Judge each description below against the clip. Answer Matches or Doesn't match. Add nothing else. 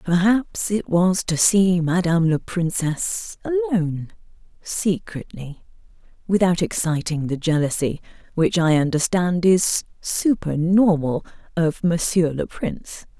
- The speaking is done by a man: Doesn't match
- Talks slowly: Matches